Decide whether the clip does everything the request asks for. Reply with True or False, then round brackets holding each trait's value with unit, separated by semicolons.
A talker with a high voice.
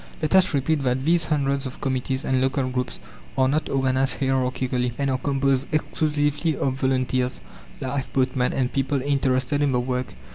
False (135 Hz)